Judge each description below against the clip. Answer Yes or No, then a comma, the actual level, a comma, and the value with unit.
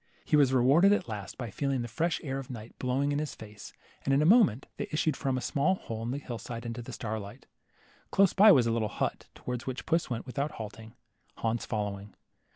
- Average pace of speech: No, fast, 230 wpm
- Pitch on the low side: Yes, low, 125 Hz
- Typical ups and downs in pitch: Yes, average, 4.2 semitones